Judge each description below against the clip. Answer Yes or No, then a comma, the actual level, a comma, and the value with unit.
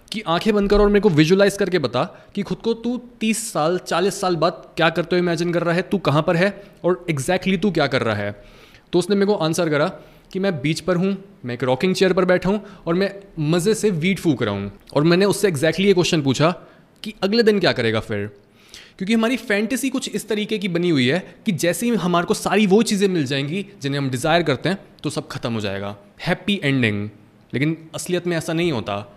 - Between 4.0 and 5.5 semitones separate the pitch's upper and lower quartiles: Yes, average, 4.9 semitones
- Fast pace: Yes, fast, 235 wpm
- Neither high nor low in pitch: Yes, medium, 175 Hz